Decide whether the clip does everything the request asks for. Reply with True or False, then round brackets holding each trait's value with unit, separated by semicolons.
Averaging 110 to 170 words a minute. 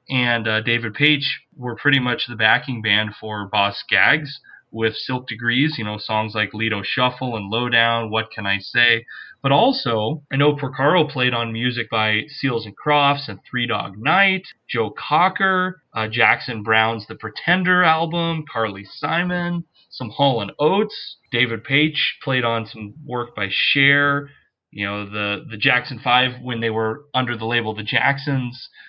True (165 wpm)